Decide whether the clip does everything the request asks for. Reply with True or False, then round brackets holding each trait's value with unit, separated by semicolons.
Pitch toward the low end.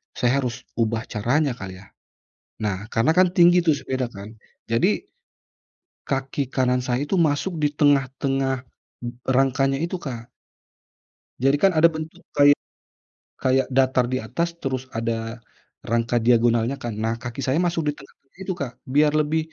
True (130 Hz)